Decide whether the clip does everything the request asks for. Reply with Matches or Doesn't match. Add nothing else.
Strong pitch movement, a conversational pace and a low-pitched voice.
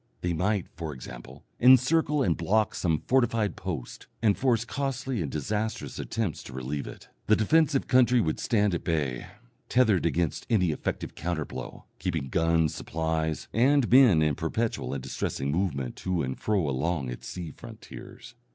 Matches